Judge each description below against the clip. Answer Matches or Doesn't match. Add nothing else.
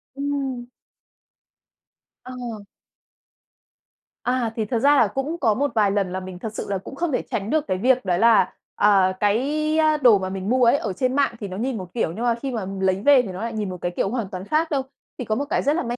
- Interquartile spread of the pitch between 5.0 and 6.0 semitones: Matches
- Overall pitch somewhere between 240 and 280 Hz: Doesn't match